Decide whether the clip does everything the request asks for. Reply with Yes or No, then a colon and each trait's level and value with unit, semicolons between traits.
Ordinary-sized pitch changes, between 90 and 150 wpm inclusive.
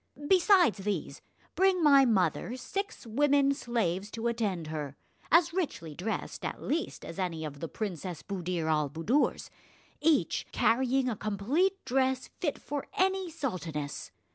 No: wide, 8.9 semitones; average, 140 wpm